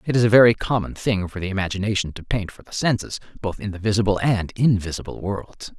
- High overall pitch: No, low, 100 Hz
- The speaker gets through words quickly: Yes, fast, 220 wpm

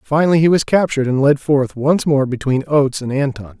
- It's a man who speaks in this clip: Yes, male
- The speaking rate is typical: No, fast, 215 wpm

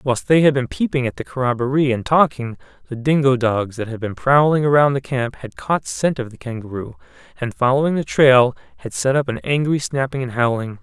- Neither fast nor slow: No, fast, 210 wpm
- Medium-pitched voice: No, low, 130 Hz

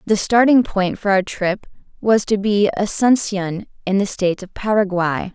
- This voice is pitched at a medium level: No, high, 200 Hz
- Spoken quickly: No, average, 170 wpm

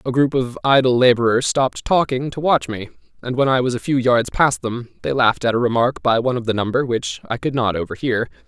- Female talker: No, male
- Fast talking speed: Yes, fast, 240 wpm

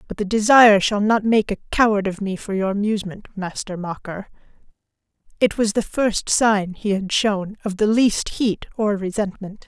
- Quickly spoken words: No, average, 180 wpm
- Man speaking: No, female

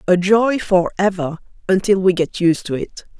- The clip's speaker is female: Yes, female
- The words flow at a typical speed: Yes, average, 170 wpm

